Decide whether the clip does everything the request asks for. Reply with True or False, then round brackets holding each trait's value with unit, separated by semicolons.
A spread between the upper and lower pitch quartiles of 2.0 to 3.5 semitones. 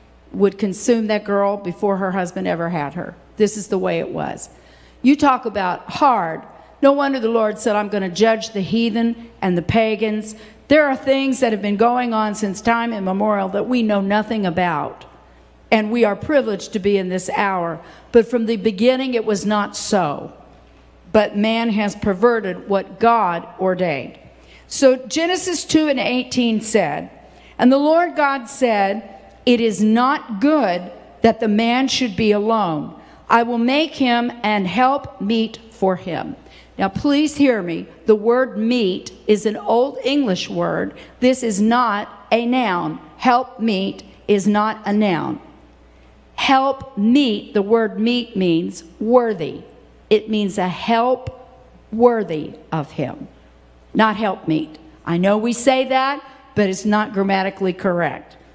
False (3.9 semitones)